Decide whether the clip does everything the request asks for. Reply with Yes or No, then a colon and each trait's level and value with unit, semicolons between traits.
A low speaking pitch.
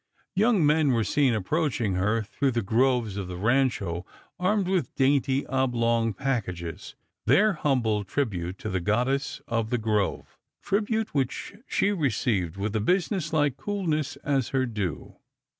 Yes: low, 125 Hz